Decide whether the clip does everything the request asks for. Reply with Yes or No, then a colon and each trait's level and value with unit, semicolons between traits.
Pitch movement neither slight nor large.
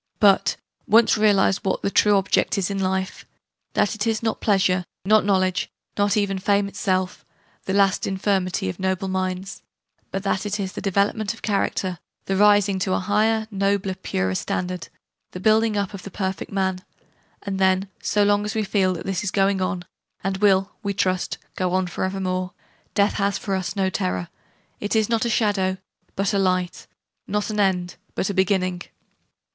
No: narrow, 1.6 semitones